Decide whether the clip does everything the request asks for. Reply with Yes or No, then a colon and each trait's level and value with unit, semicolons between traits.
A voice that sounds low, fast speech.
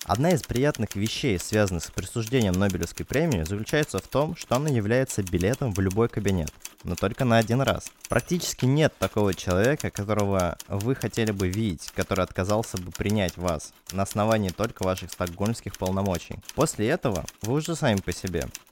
Yes: low, 105 Hz; fast, 165 wpm